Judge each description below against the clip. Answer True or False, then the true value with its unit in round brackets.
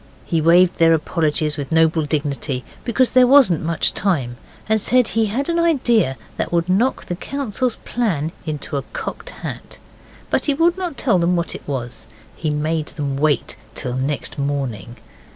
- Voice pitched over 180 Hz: False (165 Hz)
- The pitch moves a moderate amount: False (8.0 semitones)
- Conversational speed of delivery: True (170 wpm)